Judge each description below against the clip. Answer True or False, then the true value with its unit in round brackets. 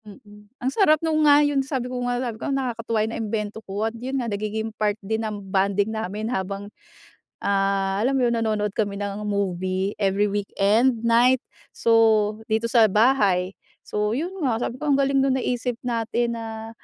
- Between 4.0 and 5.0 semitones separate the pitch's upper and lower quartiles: False (3.1 semitones)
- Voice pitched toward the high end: True (220 Hz)